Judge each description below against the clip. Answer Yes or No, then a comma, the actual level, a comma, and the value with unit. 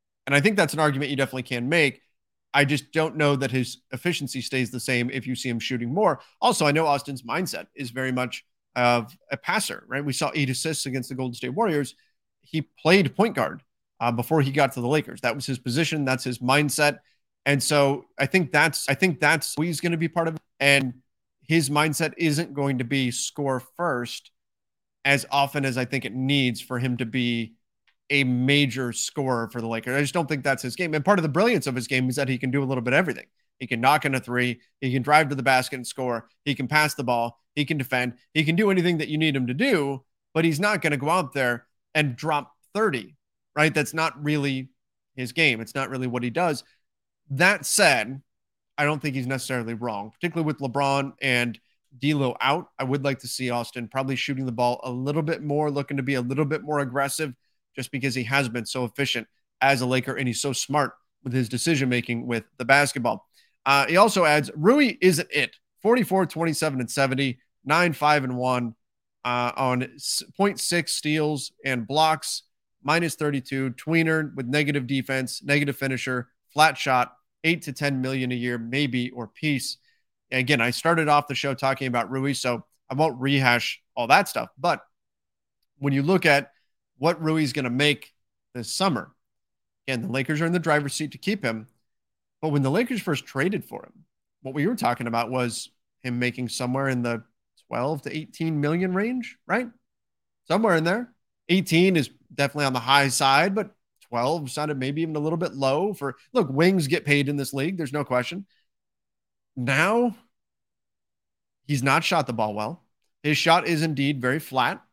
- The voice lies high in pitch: No, medium, 140 Hz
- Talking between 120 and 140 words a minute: No, fast, 205 wpm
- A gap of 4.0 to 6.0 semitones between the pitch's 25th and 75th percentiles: No, average, 3.6 semitones